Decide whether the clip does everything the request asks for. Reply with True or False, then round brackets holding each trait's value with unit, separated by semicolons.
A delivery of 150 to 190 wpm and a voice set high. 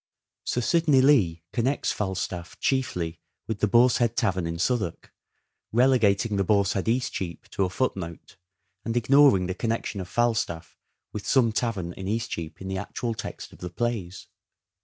False (160 wpm; 105 Hz)